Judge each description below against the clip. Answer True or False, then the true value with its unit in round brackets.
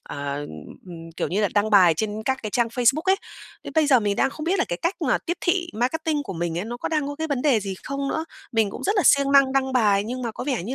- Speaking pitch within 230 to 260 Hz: True (255 Hz)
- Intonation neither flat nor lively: False (6.1 semitones)